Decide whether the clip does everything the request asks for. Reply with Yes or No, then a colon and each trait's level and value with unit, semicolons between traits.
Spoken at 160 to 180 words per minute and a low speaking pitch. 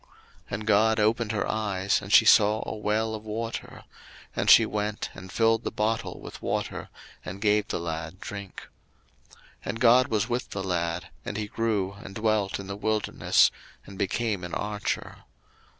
Yes: average, 175 wpm; low, 105 Hz